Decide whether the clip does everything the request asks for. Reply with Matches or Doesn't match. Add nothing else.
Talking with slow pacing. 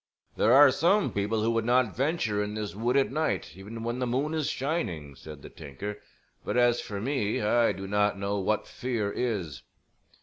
Doesn't match